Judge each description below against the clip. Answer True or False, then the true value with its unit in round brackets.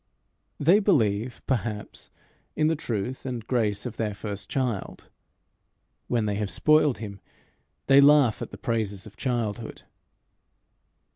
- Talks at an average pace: False (130 wpm)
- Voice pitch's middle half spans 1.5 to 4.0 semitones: False (4.5 semitones)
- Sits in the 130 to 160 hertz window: False (115 Hz)